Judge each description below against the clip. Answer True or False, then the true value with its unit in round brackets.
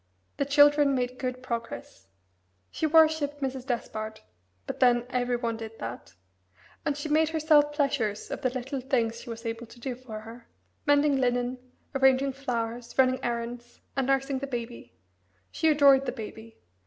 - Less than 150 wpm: False (160 wpm)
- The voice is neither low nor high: False (255 Hz)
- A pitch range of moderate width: True (3.0 semitones)